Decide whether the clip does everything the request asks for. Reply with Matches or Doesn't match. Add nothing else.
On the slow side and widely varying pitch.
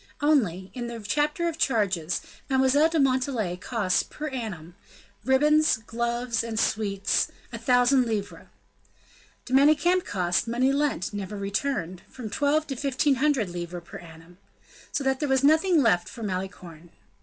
Doesn't match